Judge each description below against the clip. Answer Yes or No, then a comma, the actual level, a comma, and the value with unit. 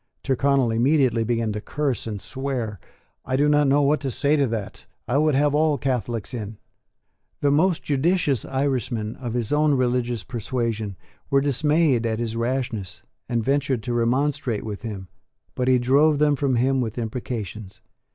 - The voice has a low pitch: Yes, low, 125 Hz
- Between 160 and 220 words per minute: Yes, average, 165 wpm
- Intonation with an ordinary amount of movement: Yes, average, 3.7 semitones